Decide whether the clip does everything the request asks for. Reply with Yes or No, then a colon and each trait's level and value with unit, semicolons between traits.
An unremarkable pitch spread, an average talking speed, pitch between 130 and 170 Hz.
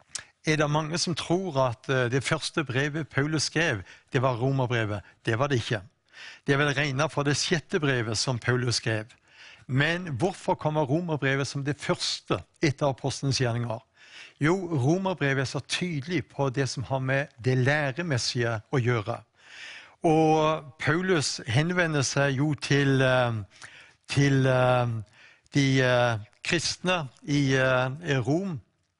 No: average, 3.6 semitones; slow, 130 wpm; medium, 140 Hz